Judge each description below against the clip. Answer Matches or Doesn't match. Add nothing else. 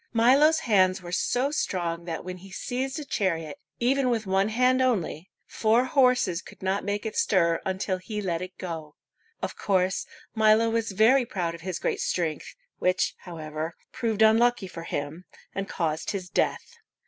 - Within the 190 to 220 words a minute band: Doesn't match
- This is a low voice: Doesn't match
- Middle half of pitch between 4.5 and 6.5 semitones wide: Matches